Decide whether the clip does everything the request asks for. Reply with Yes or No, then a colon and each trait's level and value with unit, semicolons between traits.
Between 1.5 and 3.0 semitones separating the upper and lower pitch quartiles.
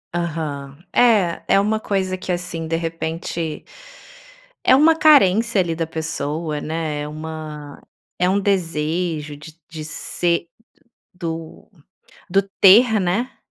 No: average, 3.6 semitones